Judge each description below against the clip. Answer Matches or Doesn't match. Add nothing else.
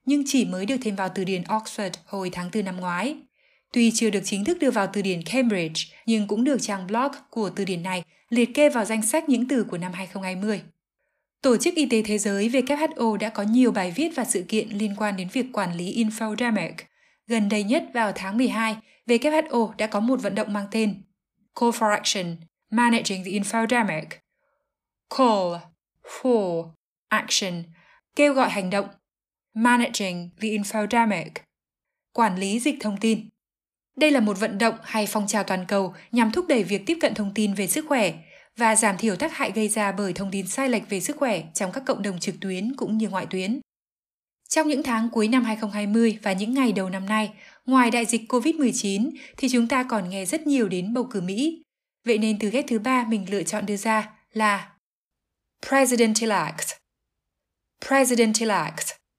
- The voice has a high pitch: Matches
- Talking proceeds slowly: Doesn't match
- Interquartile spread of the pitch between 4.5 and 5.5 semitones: Doesn't match